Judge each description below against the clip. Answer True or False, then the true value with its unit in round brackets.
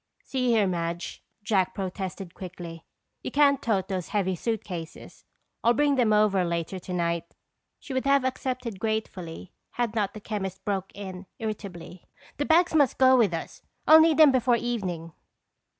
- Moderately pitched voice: False (205 Hz)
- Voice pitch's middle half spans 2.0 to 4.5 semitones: False (5.6 semitones)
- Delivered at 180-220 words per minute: False (155 wpm)